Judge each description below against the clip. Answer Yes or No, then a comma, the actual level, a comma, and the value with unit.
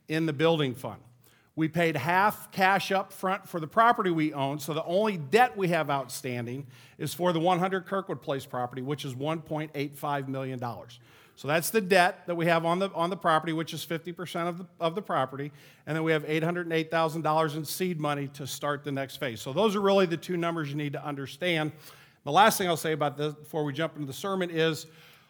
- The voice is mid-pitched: Yes, medium, 160 Hz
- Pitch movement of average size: Yes, average, 3.5 semitones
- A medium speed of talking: No, fast, 225 wpm